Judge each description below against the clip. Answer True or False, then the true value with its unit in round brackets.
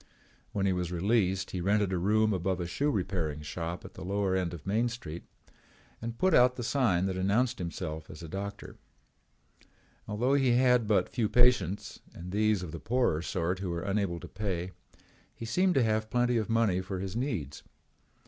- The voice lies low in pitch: True (100 Hz)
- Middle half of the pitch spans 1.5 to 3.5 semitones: False (4.4 semitones)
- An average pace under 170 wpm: False (190 wpm)